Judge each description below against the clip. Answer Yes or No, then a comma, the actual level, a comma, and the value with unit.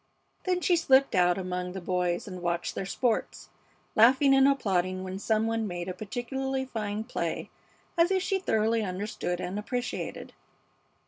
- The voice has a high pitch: Yes, high, 215 Hz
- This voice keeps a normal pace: Yes, average, 155 wpm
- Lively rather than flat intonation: Yes, wide, 6.3 semitones